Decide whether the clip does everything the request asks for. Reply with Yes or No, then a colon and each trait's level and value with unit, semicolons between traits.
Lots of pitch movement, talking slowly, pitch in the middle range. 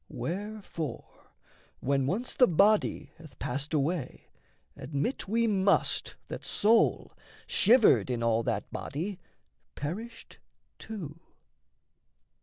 Yes: wide, 7.3 semitones; slow, 95 wpm; medium, 170 Hz